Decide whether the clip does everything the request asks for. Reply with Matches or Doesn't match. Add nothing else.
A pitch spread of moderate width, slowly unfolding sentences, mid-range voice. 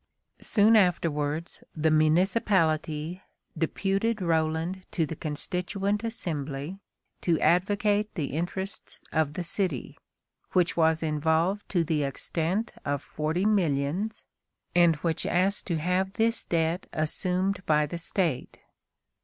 Matches